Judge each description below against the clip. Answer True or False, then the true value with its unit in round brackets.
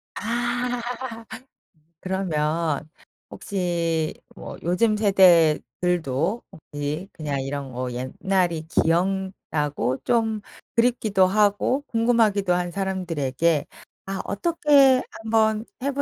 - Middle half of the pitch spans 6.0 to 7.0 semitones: False (5.6 semitones)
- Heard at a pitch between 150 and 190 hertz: True (185 Hz)